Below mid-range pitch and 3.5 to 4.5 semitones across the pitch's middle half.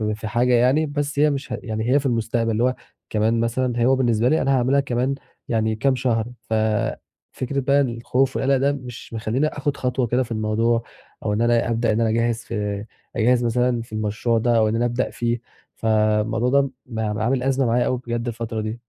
No: low, 120 Hz; narrow, 2.4 semitones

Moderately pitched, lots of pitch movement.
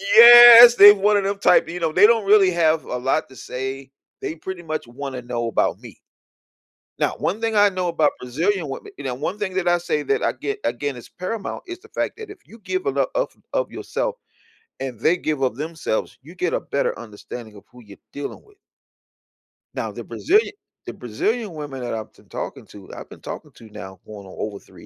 Yes: medium, 165 Hz; wide, 8.4 semitones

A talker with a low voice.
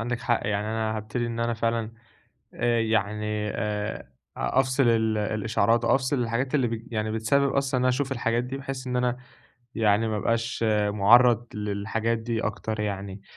Yes: low, 115 Hz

